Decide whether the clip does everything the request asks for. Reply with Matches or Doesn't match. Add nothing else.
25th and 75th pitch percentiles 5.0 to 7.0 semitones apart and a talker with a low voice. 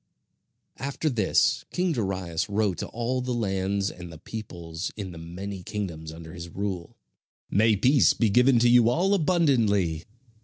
Matches